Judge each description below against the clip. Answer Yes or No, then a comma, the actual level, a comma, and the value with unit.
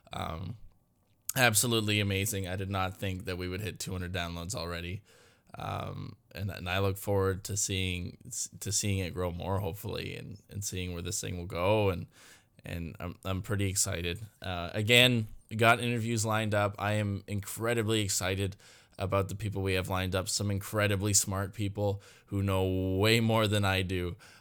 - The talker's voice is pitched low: Yes, low, 100 Hz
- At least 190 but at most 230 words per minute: No, average, 170 wpm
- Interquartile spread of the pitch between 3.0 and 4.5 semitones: No, narrow, 2.4 semitones